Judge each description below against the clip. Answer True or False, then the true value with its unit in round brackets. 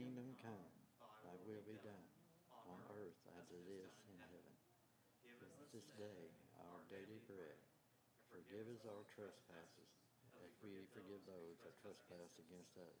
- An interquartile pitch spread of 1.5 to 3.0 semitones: False (3.8 semitones)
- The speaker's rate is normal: True (150 wpm)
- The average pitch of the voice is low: True (100 Hz)